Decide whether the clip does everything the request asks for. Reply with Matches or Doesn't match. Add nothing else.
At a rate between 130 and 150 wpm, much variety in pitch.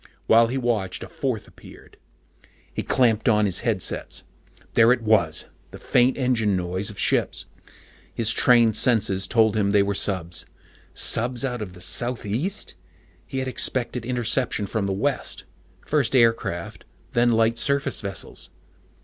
Doesn't match